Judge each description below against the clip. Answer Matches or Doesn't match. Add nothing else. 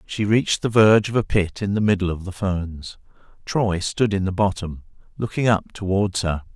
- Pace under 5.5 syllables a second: Matches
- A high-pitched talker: Doesn't match